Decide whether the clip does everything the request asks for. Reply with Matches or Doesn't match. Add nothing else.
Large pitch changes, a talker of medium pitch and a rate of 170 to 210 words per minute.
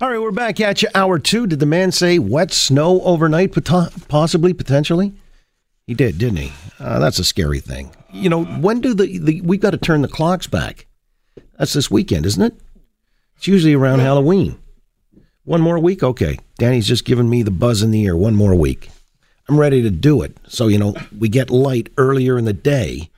Matches